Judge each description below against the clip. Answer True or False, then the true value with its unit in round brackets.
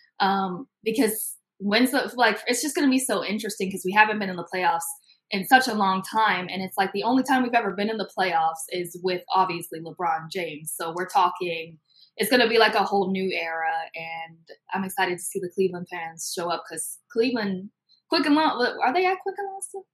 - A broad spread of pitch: False (4.8 semitones)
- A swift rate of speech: True (225 wpm)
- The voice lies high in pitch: True (195 Hz)